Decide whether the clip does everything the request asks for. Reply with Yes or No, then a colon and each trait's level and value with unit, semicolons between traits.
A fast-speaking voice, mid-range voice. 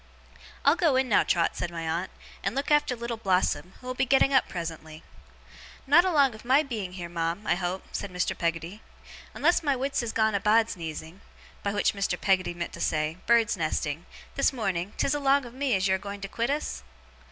No: fast, 210 wpm; high, 205 Hz